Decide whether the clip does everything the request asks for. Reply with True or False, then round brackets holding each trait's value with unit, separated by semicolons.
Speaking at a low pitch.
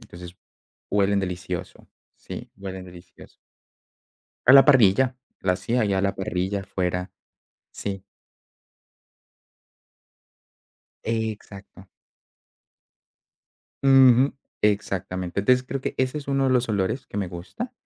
True (100 Hz)